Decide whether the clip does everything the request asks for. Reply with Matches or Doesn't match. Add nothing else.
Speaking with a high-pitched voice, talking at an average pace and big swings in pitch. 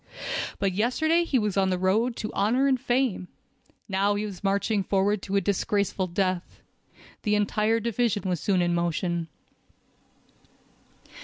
Doesn't match